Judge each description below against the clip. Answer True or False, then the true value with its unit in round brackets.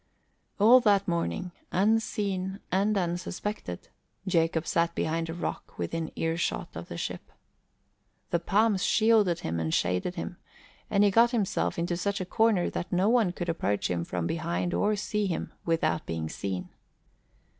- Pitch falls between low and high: True (180 Hz)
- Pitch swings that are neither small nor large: True (3.9 semitones)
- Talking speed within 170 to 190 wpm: False (155 wpm)